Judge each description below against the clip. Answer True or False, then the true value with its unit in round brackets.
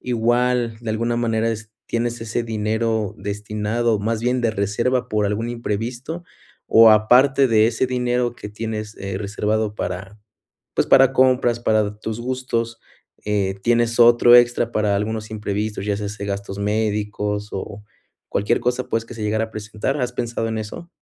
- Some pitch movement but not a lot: False (2.3 semitones)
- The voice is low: True (110 Hz)